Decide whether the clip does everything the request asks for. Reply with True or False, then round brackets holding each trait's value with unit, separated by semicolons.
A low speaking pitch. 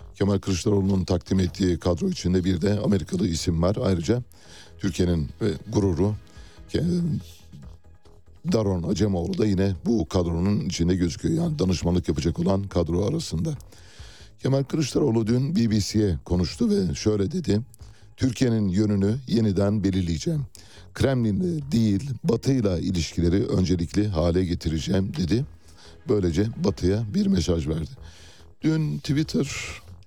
True (95 Hz)